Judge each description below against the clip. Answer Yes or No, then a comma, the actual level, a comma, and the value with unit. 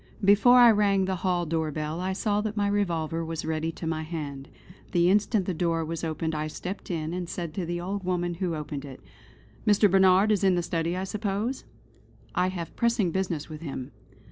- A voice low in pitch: No, medium, 175 Hz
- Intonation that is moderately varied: Yes, average, 3.5 semitones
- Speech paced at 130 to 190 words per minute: No, fast, 205 wpm